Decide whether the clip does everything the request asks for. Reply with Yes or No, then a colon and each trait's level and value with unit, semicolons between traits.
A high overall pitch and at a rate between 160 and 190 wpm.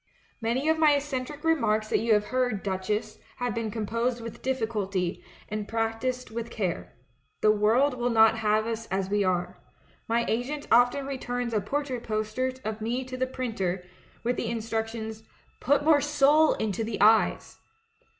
Yes: high, 230 Hz; average, 170 wpm